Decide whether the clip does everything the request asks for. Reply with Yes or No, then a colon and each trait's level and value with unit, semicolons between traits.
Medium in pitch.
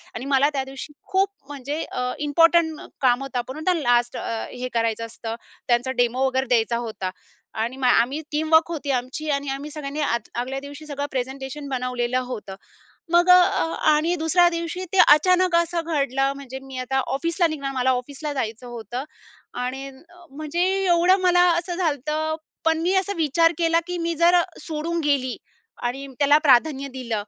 No: very high, 280 Hz